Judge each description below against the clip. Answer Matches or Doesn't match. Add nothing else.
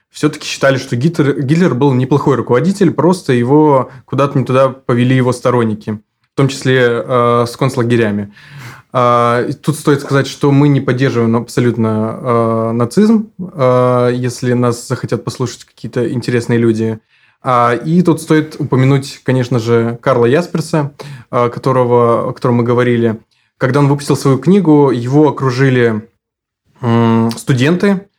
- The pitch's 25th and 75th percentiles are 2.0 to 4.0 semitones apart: Matches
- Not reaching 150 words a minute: Matches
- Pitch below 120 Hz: Doesn't match